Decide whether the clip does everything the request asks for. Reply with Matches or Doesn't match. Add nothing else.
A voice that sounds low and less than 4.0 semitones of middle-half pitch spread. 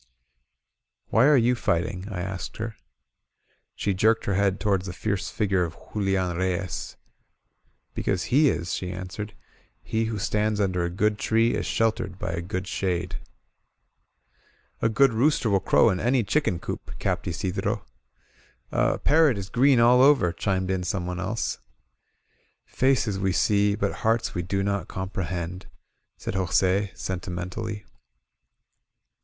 Matches